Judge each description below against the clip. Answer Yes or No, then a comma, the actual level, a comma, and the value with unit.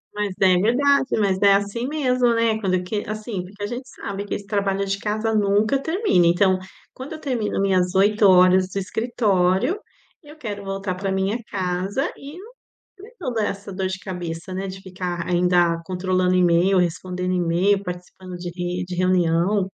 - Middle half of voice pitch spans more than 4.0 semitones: No, average, 3.0 semitones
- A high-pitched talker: Yes, high, 195 Hz